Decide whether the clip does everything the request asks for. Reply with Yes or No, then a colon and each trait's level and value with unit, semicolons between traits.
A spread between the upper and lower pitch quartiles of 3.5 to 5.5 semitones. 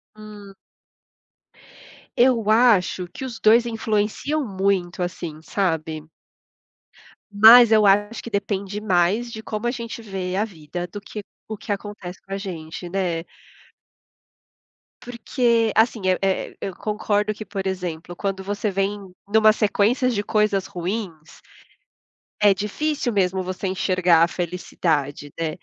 No: average, 3.1 semitones